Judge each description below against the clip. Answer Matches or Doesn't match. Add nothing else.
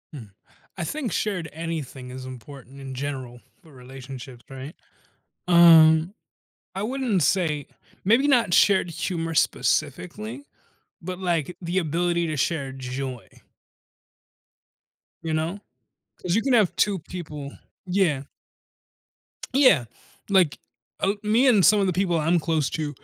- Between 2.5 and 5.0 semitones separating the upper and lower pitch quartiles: Doesn't match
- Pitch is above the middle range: Doesn't match